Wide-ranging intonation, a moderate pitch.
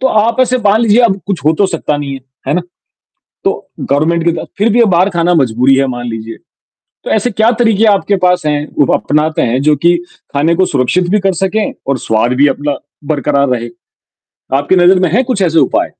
Yes: wide, 5.7 semitones; medium, 165 Hz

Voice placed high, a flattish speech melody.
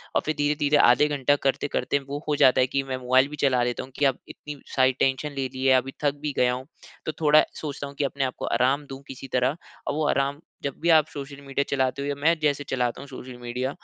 No: medium, 140 Hz; narrow, 1.9 semitones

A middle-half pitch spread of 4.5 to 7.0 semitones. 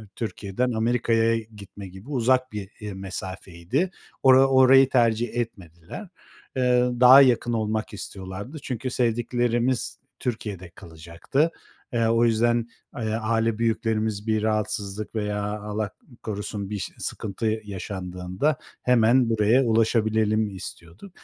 No: average, 3.0 semitones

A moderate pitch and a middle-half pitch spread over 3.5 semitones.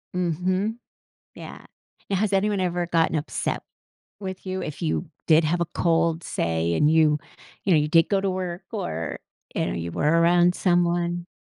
No: medium, 175 Hz; narrow, 2.6 semitones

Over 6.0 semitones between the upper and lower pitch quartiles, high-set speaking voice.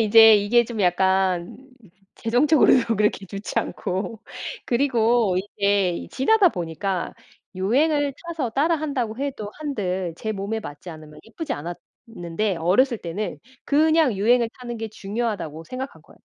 No: average, 5.1 semitones; high, 220 Hz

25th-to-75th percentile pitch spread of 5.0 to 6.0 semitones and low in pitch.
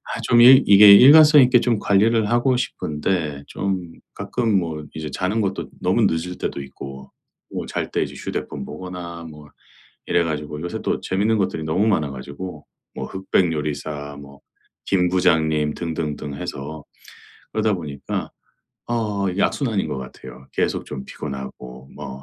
Yes: wide, 5.5 semitones; very low, 85 Hz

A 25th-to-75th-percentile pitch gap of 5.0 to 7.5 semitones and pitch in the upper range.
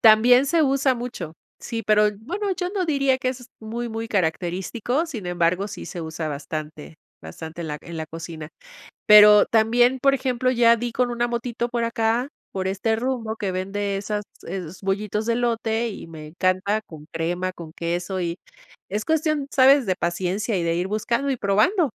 Yes: wide, 5.5 semitones; high, 215 Hz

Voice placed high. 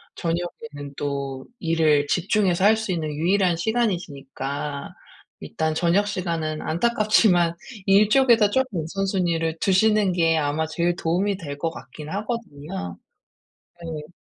No: medium, 170 Hz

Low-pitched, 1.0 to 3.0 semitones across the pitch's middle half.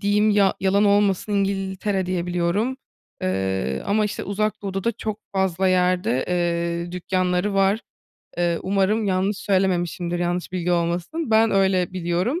No: high, 190 Hz; narrow, 2.4 semitones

